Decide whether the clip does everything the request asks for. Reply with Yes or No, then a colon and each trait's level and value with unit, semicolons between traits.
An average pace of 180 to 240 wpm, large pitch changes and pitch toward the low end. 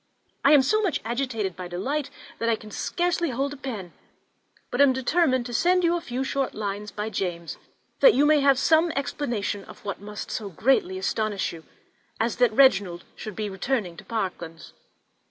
No: average, 185 wpm; wide, 5.7 semitones; high, 235 Hz